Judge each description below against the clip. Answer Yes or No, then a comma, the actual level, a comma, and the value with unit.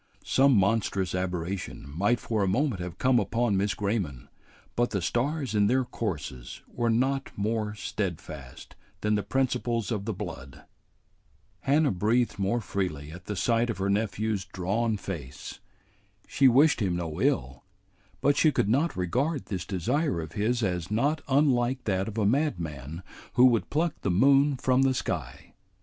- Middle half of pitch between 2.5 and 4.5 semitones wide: No, wide, 5.6 semitones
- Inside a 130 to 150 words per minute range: No, average, 160 wpm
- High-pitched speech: No, low, 105 Hz